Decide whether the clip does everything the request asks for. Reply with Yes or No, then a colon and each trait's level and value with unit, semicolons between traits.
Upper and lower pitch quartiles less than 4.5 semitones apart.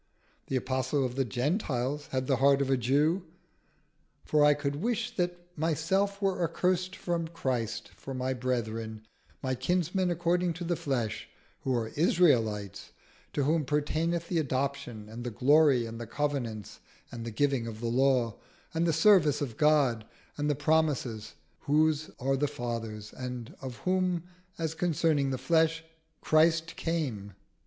No: average, 4.9 semitones